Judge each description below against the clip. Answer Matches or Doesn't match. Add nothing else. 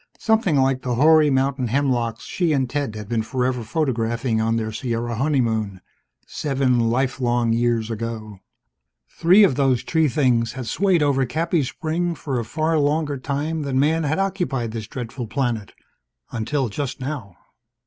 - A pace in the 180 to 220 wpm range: Doesn't match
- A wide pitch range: Doesn't match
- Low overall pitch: Matches